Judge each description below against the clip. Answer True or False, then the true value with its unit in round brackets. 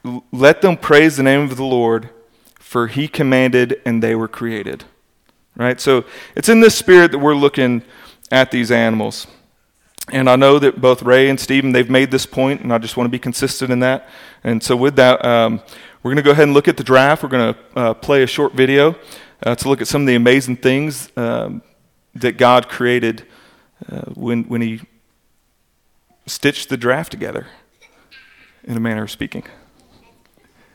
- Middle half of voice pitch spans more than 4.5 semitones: False (2.5 semitones)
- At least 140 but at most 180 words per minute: False (190 wpm)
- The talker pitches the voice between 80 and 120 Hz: False (130 Hz)